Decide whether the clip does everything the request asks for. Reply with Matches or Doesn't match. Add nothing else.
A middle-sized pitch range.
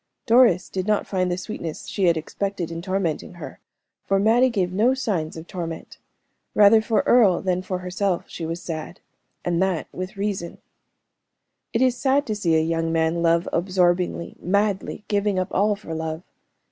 Matches